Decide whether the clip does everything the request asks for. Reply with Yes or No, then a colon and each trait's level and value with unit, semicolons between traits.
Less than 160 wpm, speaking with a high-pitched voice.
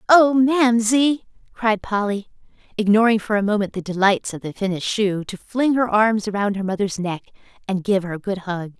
No: average, 190 wpm; high, 210 Hz